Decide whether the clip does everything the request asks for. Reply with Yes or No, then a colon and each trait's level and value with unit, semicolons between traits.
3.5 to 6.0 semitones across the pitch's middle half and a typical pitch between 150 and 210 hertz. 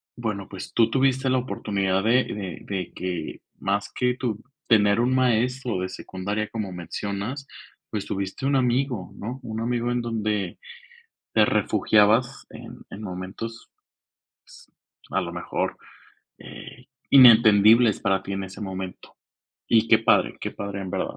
No: average, 3.8 semitones; low, 110 Hz